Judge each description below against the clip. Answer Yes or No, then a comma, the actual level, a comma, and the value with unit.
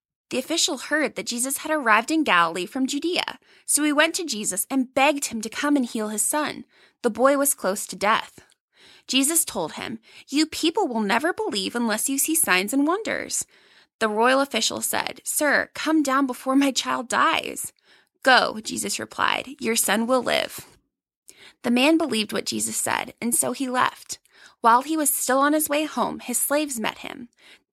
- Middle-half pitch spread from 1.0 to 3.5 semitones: No, average, 4.6 semitones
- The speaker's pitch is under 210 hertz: No, very high, 270 Hz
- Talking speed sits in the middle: Yes, average, 185 wpm